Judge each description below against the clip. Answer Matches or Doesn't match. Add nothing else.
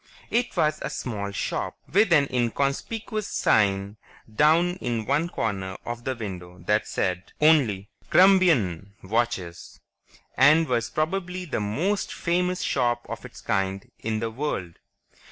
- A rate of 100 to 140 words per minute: Matches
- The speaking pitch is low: Matches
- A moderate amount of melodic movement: Doesn't match